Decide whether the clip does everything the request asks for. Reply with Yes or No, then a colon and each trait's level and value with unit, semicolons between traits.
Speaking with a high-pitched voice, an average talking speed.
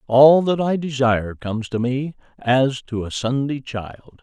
No: low, 130 Hz; average, 170 wpm